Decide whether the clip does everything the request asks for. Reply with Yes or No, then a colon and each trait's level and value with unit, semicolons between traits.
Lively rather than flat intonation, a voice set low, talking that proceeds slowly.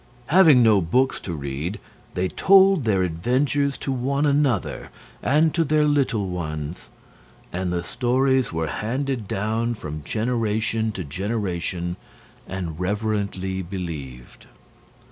Yes: wide, 6.9 semitones; low, 105 Hz; slow, 120 wpm